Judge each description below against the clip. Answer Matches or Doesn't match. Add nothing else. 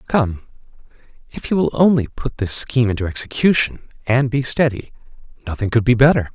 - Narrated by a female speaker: Doesn't match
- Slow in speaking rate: Doesn't match